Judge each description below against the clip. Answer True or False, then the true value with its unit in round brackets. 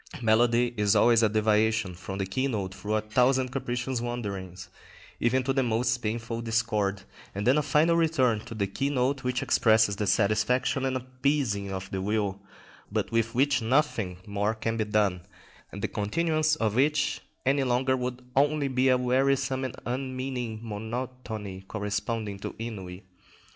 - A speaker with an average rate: True (160 wpm)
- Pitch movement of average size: True (3.8 semitones)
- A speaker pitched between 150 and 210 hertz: False (115 Hz)